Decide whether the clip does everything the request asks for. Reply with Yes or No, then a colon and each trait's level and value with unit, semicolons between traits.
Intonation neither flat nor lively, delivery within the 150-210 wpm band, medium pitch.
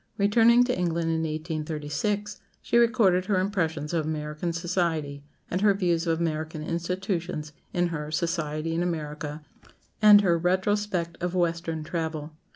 No: average, 3.0 semitones; average, 140 wpm; medium, 170 Hz